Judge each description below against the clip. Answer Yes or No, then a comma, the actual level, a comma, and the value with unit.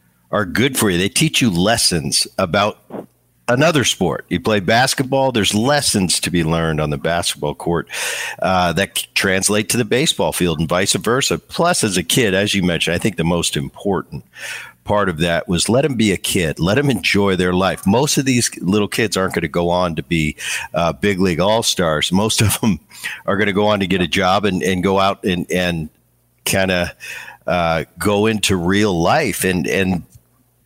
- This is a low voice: Yes, very low, 95 Hz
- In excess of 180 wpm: Yes, average, 200 wpm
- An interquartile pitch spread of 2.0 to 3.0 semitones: No, average, 3.8 semitones